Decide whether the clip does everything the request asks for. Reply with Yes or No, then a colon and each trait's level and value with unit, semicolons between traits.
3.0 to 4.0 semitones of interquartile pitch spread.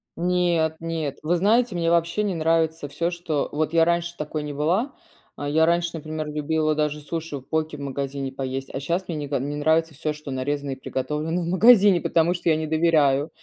No: narrow, 2.6 semitones